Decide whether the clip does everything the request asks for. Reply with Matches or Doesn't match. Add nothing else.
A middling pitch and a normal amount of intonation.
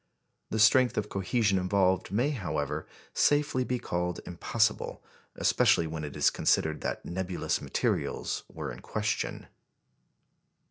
Doesn't match